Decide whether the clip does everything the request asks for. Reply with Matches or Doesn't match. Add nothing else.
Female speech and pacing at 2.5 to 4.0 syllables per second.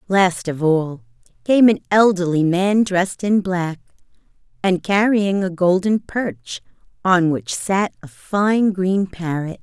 Matches